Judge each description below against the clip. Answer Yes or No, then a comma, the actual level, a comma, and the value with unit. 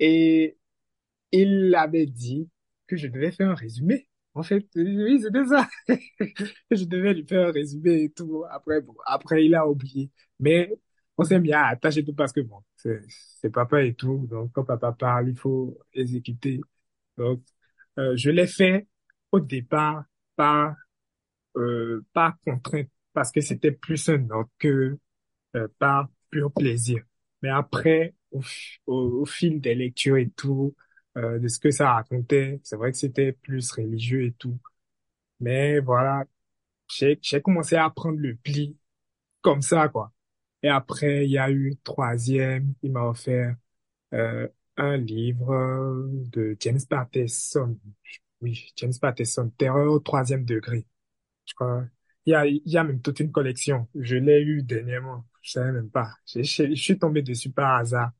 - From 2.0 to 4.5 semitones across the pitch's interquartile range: Yes, average, 3.8 semitones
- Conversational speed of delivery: Yes, average, 160 wpm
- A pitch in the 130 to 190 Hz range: Yes, low, 135 Hz